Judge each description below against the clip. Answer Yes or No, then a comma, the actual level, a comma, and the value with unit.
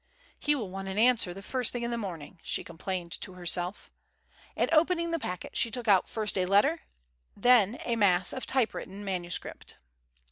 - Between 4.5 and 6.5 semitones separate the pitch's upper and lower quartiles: Yes, average, 5.1 semitones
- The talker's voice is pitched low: No, high, 205 Hz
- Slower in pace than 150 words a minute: No, average, 185 wpm